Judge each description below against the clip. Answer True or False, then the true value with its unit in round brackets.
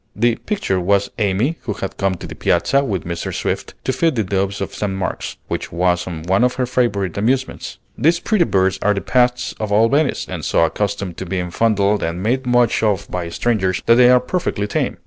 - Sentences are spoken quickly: True (210 wpm)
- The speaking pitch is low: True (105 Hz)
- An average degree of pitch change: True (4.6 semitones)